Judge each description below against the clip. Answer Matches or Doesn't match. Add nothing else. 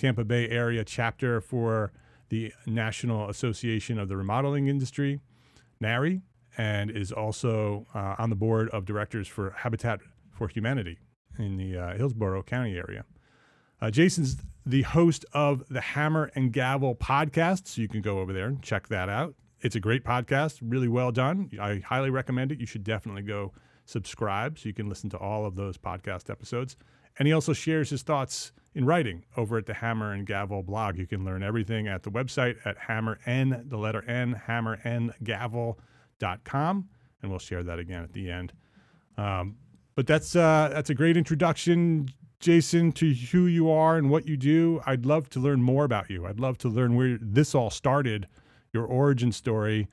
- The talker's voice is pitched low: Matches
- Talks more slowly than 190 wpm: Matches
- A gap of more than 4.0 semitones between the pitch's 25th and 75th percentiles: Matches